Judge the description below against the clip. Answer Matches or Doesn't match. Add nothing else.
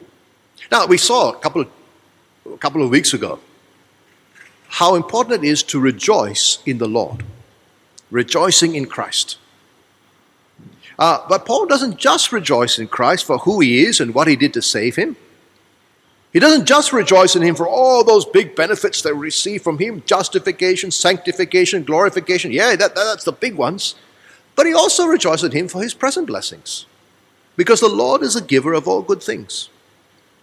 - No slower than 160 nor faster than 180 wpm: Matches